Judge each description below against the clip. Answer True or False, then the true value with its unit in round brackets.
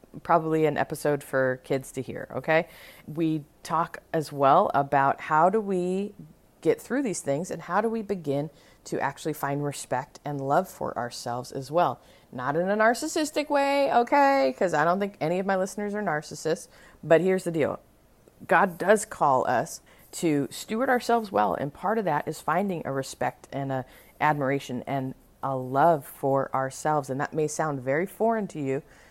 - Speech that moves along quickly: False (180 wpm)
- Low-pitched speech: False (155 Hz)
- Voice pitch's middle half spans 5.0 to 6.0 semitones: True (5.5 semitones)